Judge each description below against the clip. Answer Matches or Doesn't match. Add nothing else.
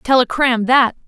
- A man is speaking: Doesn't match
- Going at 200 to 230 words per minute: Matches